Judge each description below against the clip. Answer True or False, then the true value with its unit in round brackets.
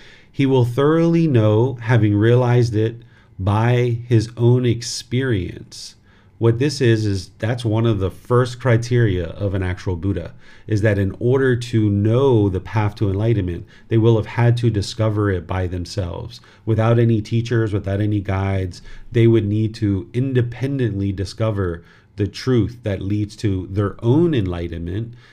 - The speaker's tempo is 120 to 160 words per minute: True (150 wpm)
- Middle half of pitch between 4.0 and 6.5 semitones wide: False (3.0 semitones)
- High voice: False (110 Hz)